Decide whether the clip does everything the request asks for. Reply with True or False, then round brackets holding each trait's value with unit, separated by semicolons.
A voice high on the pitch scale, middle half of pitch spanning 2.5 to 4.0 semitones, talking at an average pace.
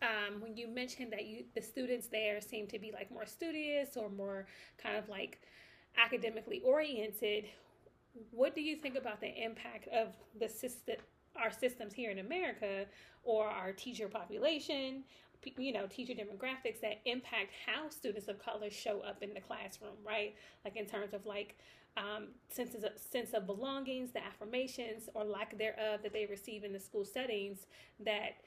True (220 Hz; 3.0 semitones; 170 wpm)